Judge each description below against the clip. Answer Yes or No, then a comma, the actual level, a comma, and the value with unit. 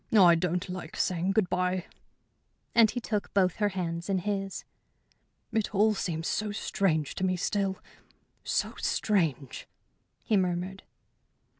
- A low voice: No, medium, 185 Hz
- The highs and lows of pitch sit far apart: No, average, 2.7 semitones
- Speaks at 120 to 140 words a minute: Yes, slow, 135 wpm